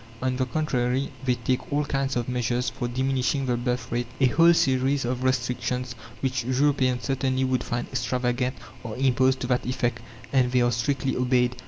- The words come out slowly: No, average, 180 wpm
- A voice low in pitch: Yes, low, 125 Hz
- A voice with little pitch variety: Yes, narrow, 1.3 semitones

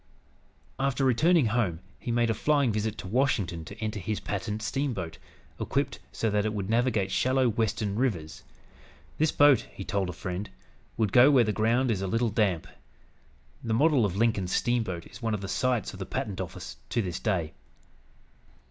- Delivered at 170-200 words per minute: Yes, average, 180 wpm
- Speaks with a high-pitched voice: No, low, 110 Hz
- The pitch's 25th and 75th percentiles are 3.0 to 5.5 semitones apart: Yes, average, 3.9 semitones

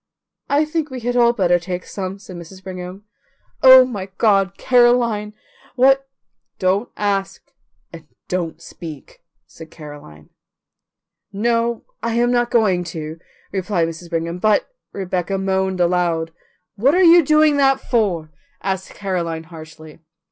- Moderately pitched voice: No, high, 195 Hz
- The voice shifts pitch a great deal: Yes, wide, 5.7 semitones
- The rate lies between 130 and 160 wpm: Yes, average, 140 wpm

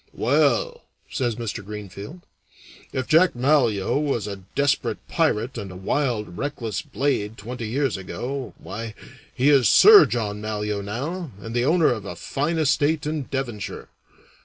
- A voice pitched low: Yes, low, 120 Hz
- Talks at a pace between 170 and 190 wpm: No, average, 145 wpm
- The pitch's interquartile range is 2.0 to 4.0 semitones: No, wide, 5.5 semitones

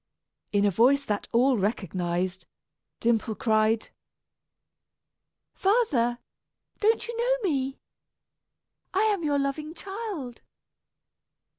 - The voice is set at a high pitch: Yes, very high, 265 Hz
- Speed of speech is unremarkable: No, slow, 95 wpm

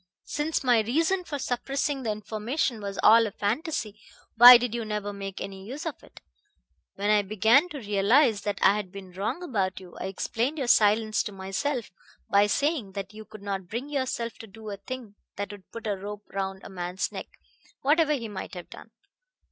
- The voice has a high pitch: Yes, high, 215 Hz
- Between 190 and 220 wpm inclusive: Yes, average, 195 wpm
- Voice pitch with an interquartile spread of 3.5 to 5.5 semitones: Yes, average, 4.4 semitones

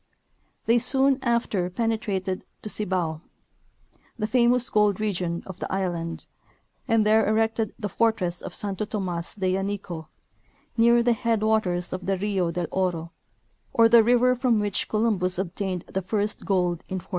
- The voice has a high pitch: Yes, high, 205 Hz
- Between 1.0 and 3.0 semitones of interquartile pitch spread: No, average, 3.7 semitones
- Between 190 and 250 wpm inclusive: No, average, 155 wpm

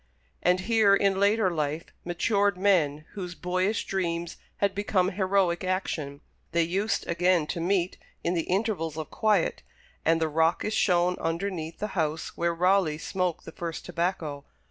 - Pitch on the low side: No, medium, 180 Hz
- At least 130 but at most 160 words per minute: Yes, average, 155 wpm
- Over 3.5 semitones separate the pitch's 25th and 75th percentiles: No, average, 3.1 semitones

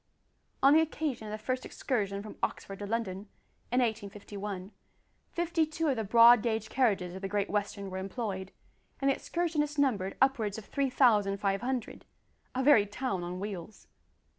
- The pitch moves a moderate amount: Yes, average, 4.9 semitones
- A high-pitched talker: Yes, high, 215 Hz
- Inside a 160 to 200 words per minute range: Yes, average, 170 wpm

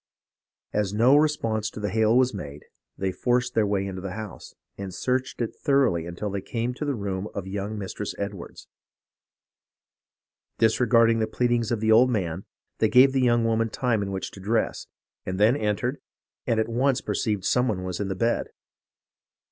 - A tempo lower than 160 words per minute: No, average, 180 wpm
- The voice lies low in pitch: Yes, low, 110 Hz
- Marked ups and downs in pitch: No, average, 3.5 semitones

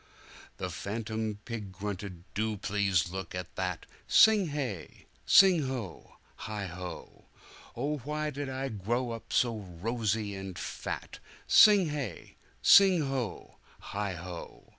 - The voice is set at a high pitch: No, low, 110 Hz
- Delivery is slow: Yes, slow, 115 wpm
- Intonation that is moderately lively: No, wide, 5.9 semitones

